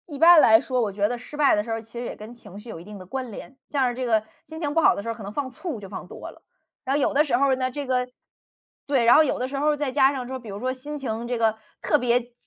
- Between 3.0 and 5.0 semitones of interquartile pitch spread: Yes, average, 3.7 semitones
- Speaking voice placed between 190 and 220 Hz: No, very high, 250 Hz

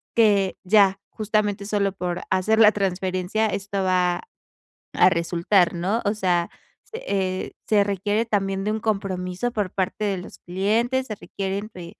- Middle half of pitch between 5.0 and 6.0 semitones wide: No, narrow, 2.4 semitones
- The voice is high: Yes, high, 195 Hz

